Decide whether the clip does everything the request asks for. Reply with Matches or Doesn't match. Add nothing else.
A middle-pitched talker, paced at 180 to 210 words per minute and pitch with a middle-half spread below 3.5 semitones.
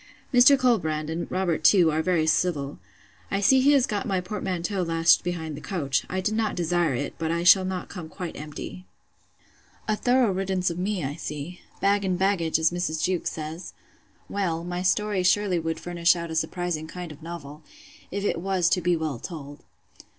Matches